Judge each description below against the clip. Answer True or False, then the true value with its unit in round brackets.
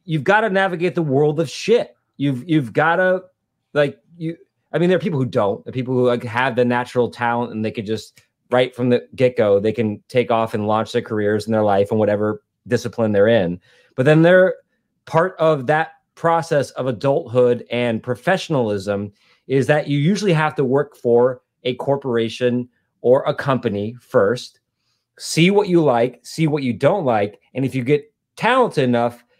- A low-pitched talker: True (125 Hz)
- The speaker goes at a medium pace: True (190 wpm)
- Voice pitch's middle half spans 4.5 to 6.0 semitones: True (5.1 semitones)